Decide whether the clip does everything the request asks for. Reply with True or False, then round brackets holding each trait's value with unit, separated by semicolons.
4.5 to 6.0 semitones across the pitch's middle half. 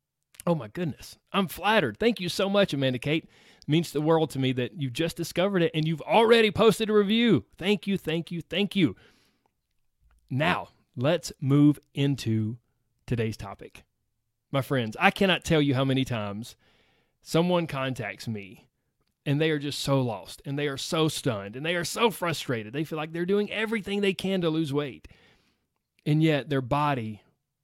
True (5.2 semitones)